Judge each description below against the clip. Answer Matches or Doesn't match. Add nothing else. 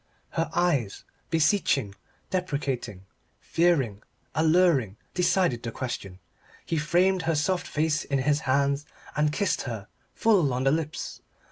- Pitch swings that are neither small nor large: Matches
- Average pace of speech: Doesn't match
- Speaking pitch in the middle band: Matches